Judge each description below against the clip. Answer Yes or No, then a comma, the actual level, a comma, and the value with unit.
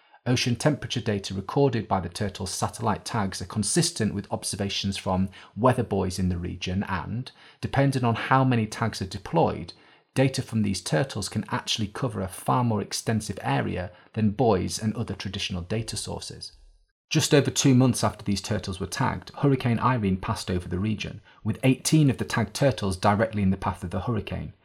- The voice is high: No, low, 105 Hz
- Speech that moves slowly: No, average, 180 wpm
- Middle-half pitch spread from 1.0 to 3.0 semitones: No, average, 3.8 semitones